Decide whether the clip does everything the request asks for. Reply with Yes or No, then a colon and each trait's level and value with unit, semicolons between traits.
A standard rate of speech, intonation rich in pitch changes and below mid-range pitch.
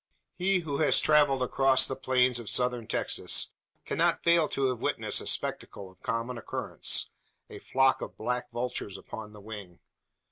No: average, 165 wpm; average, 3.0 semitones; low, 125 Hz